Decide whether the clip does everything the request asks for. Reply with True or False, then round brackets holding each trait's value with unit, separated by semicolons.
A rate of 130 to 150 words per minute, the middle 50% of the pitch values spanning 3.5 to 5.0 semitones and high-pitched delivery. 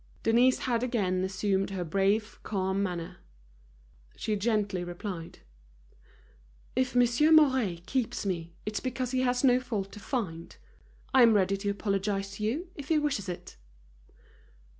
True (140 wpm; 4.6 semitones; 210 Hz)